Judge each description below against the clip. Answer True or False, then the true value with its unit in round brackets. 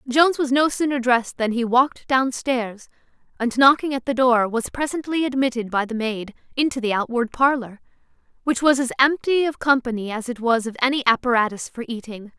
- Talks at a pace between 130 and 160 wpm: False (185 wpm)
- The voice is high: True (250 Hz)